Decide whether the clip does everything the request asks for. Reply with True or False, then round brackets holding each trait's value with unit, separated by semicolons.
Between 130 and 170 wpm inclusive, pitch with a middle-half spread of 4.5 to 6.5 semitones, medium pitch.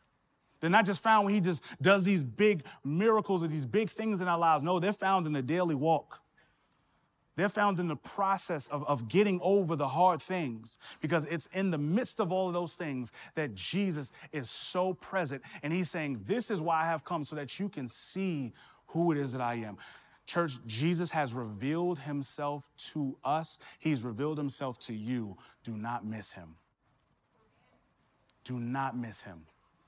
False (185 wpm; 5.6 semitones; 155 Hz)